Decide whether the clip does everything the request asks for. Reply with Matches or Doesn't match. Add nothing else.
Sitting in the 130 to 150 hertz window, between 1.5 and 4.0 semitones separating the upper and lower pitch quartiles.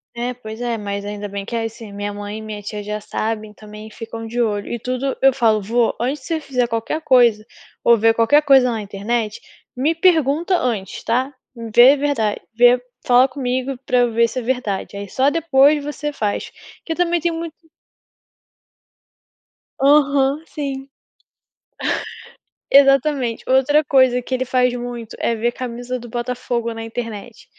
Doesn't match